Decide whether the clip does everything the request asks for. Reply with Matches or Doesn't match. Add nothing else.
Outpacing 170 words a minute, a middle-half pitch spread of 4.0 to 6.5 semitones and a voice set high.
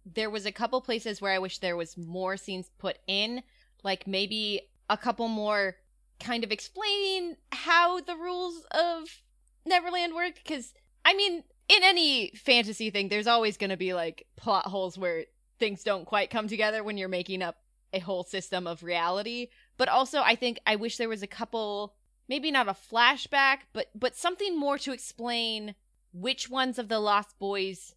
Matches